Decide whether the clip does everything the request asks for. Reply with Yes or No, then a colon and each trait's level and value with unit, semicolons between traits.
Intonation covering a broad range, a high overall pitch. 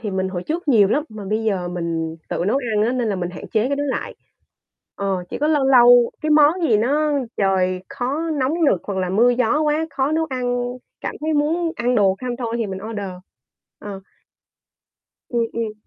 Yes: wide, 6.8 semitones; high, 235 Hz